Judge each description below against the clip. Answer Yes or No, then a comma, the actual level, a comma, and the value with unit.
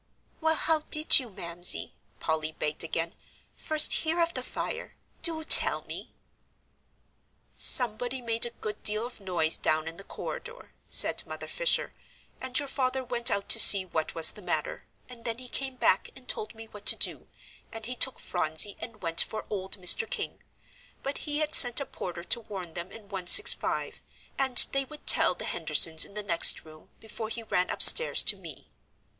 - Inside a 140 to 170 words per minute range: No, average, 185 wpm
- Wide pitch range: Yes, wide, 6.9 semitones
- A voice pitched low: No, high, 225 Hz